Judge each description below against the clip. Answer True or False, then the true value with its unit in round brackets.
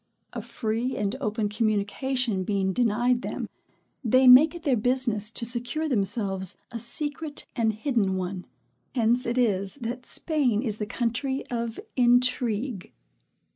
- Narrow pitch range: False (3.3 semitones)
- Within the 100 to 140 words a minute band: True (135 wpm)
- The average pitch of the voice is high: True (235 Hz)